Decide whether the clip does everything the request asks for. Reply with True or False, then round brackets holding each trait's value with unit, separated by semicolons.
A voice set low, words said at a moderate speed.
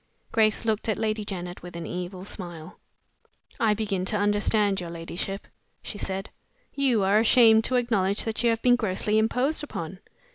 False (210 Hz; 170 wpm)